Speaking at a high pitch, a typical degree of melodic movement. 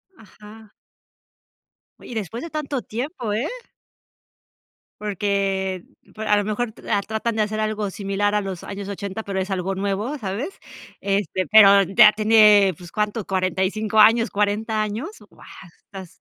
No: high, 210 Hz; narrow, 1.9 semitones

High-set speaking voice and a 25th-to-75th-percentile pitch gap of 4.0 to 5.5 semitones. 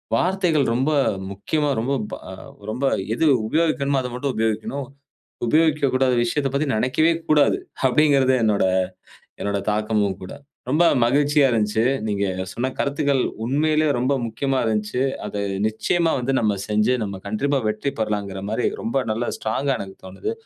No: low, 130 Hz; average, 4.9 semitones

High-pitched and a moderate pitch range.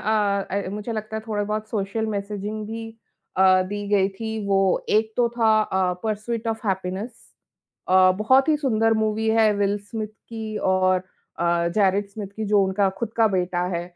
No: high, 210 Hz; narrow, 2.3 semitones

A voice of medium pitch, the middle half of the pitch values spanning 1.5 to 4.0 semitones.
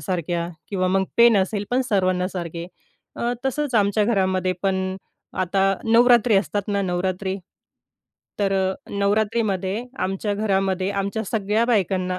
No: high, 195 Hz; narrow, 2.4 semitones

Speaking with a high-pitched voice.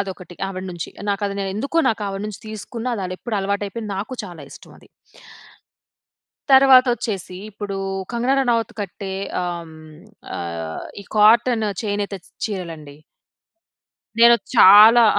Yes: high, 205 Hz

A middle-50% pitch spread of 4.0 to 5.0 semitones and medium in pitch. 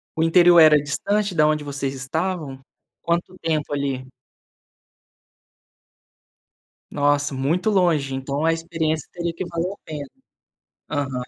No: average, 3.3 semitones; medium, 155 Hz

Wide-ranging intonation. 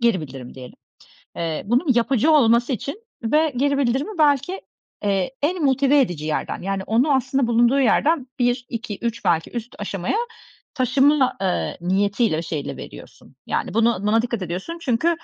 Yes: wide, 5.9 semitones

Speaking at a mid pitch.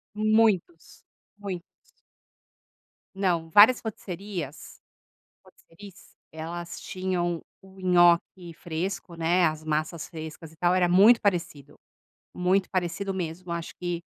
Yes: medium, 175 Hz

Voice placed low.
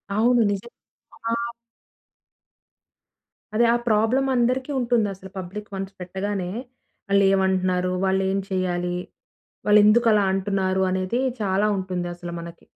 No: high, 195 Hz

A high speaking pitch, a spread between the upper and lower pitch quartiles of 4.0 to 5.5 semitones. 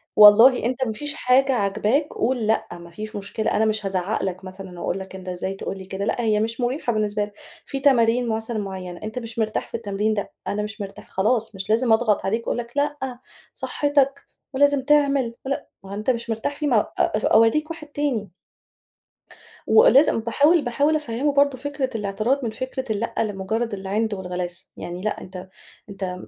Yes: high, 225 Hz; average, 4.6 semitones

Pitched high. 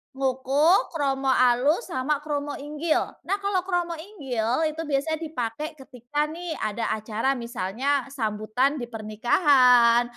Yes: very high, 275 Hz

